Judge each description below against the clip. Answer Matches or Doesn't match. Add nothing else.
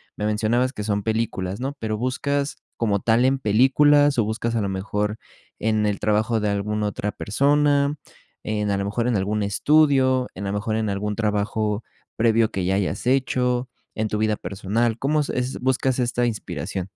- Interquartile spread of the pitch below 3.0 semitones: Doesn't match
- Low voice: Matches